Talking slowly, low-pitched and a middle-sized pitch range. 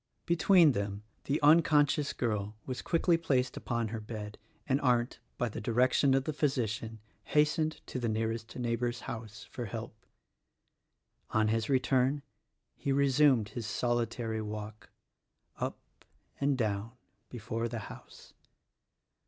Yes: slow, 130 wpm; low, 120 Hz; average, 3.8 semitones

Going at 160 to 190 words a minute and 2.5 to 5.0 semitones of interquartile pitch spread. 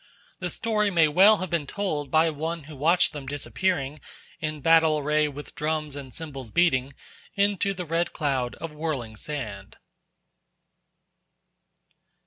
No: slow, 135 wpm; average, 3.1 semitones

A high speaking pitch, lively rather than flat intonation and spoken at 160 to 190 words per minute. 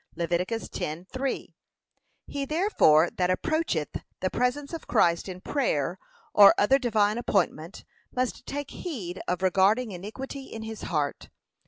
No: high, 205 Hz; wide, 6.9 semitones; slow, 135 wpm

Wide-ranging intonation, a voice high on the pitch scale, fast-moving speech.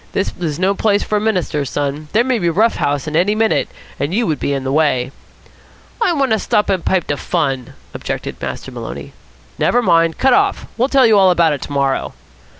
No: wide, 7.1 semitones; medium, 175 Hz; fast, 230 wpm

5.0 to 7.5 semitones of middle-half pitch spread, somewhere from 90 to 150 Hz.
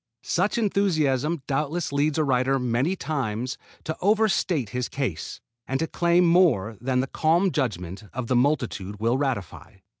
Yes: average, 5.3 semitones; low, 135 Hz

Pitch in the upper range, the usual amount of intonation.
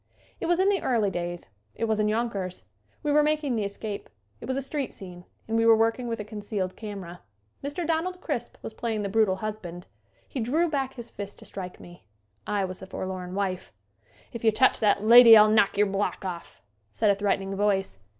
Yes: high, 210 Hz; average, 3.8 semitones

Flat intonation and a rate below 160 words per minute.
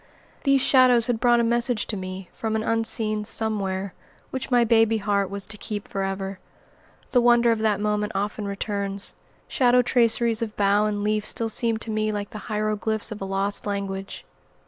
No: narrow, 2.3 semitones; average, 180 wpm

